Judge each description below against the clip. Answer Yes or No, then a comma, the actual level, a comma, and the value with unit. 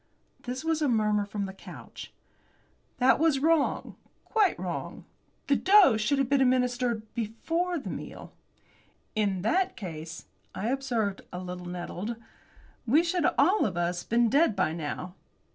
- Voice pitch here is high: Yes, high, 235 Hz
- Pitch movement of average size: No, wide, 7.0 semitones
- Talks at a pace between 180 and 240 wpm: No, average, 145 wpm